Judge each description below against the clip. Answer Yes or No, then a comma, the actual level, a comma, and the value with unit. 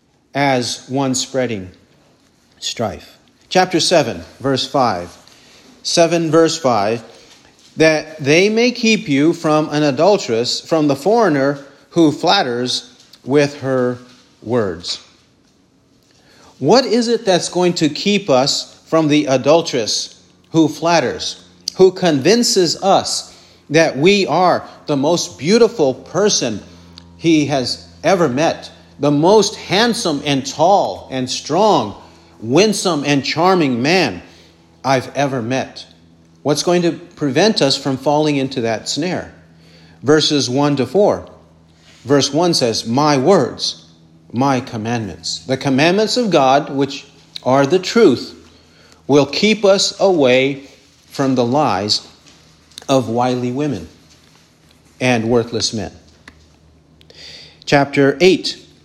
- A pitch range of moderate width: No, wide, 6.3 semitones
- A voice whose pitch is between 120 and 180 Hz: Yes, low, 135 Hz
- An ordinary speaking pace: No, slow, 115 wpm